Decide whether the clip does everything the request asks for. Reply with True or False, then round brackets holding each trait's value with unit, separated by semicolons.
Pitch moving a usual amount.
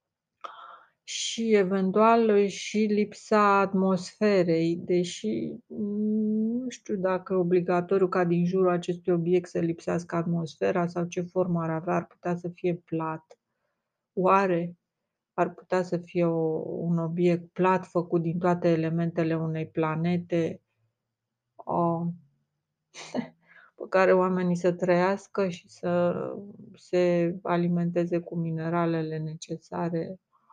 False (1.9 semitones)